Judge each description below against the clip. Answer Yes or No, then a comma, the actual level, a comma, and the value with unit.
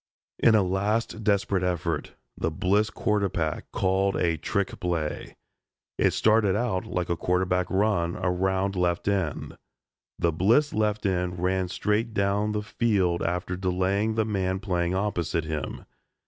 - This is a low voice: Yes, very low, 95 Hz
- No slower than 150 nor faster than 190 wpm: No, average, 140 wpm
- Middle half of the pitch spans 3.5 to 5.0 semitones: No, average, 2.7 semitones